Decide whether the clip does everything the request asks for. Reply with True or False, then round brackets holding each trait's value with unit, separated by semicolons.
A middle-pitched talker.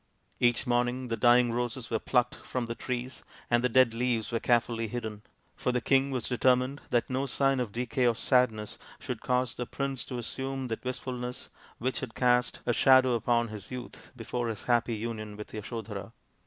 False (120 Hz)